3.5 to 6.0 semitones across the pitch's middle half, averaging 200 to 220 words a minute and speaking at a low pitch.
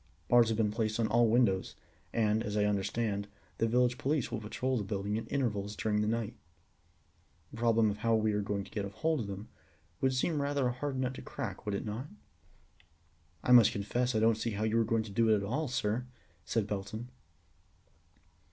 No: average, 2.8 semitones; fast, 205 wpm; low, 110 Hz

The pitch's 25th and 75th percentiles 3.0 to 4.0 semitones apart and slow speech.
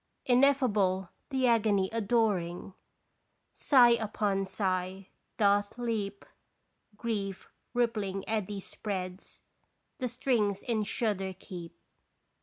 Yes: average, 3.3 semitones; slow, 85 wpm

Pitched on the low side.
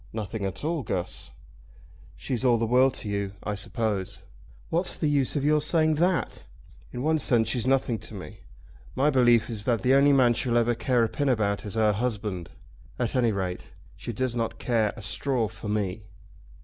Yes: low, 120 Hz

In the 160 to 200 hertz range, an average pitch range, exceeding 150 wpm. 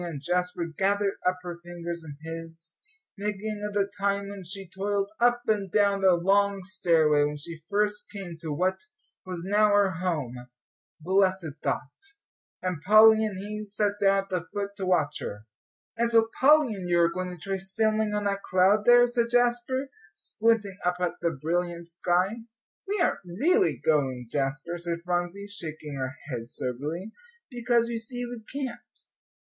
Yes: high, 190 Hz; average, 3.7 semitones; average, 170 wpm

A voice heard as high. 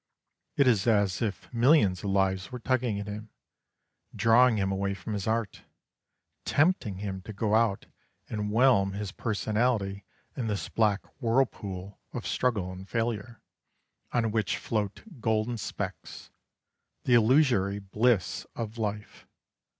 No: low, 105 Hz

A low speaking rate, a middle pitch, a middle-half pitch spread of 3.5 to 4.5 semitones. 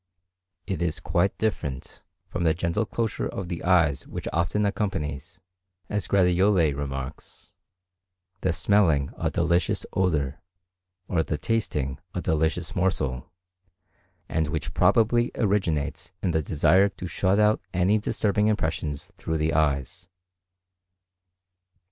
No: slow, 120 wpm; very low, 85 Hz; average, 4.1 semitones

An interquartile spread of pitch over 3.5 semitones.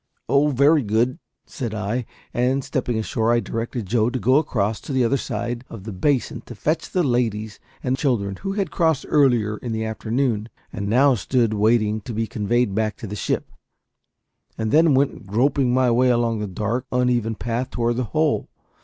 No: average, 3.1 semitones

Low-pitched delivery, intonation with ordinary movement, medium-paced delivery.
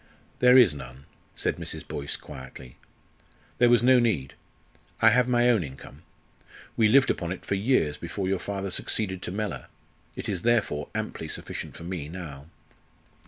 No: very low, 95 Hz; wide, 8.0 semitones; average, 165 wpm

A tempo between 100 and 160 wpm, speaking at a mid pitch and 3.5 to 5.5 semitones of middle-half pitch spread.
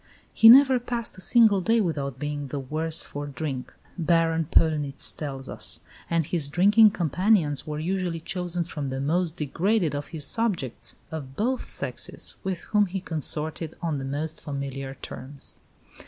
Yes: average, 155 wpm; medium, 160 Hz; average, 4.5 semitones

